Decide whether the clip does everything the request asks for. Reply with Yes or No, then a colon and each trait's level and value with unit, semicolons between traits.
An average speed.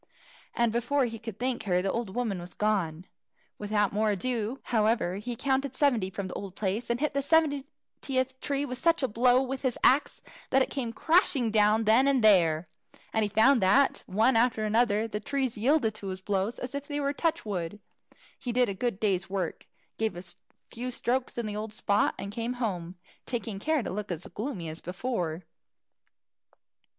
Yes: average, 190 wpm